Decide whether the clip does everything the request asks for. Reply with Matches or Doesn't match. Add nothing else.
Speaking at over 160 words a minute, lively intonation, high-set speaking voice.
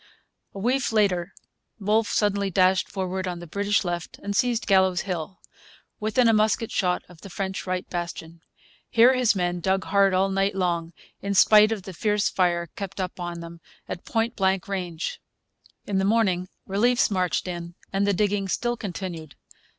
Doesn't match